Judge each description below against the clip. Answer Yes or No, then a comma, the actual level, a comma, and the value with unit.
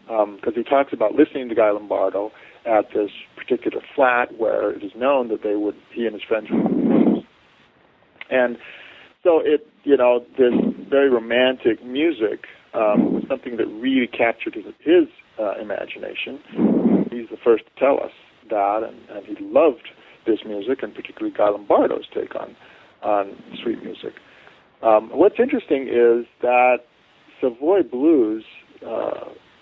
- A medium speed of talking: Yes, average, 160 wpm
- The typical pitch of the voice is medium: Yes, medium, 150 Hz